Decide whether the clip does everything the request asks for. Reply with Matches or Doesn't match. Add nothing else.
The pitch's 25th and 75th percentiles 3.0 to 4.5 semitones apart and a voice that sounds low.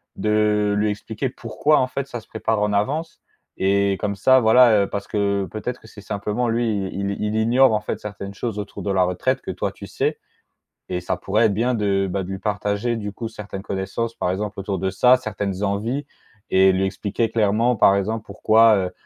Doesn't match